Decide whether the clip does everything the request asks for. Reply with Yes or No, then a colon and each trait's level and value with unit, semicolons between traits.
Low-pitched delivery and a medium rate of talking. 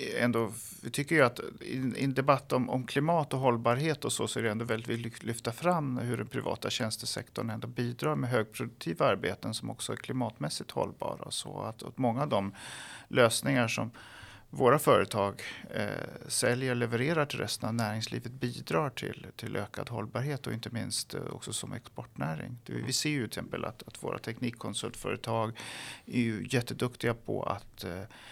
Yes: low, 120 Hz; average, 175 wpm